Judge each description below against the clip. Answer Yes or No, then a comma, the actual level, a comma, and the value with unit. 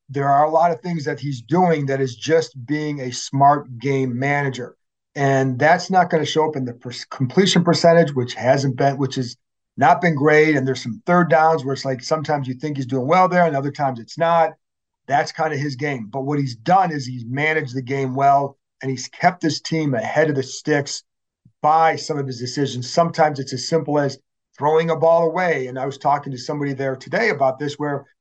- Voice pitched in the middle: Yes, medium, 145 Hz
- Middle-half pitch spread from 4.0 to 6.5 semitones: No, average, 3.1 semitones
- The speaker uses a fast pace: Yes, fast, 225 wpm